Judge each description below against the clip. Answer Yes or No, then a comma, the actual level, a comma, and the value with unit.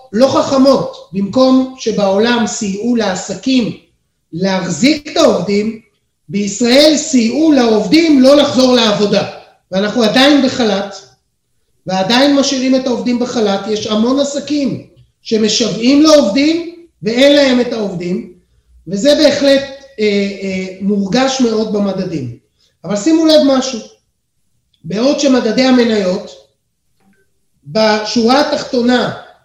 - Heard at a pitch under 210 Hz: No, high, 230 Hz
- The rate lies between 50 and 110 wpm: Yes, slow, 100 wpm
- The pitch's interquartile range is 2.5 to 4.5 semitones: No, wide, 5.6 semitones